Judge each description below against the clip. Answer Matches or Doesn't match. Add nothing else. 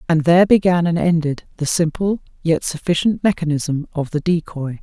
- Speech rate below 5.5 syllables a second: Matches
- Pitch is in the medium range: Matches